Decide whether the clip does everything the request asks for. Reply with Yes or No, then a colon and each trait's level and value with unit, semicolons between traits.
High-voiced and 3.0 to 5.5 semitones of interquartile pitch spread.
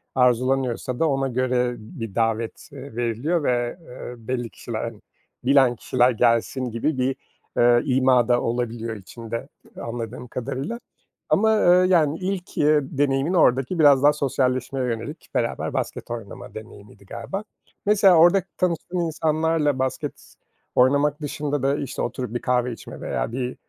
No: low, 130 Hz; average, 3.7 semitones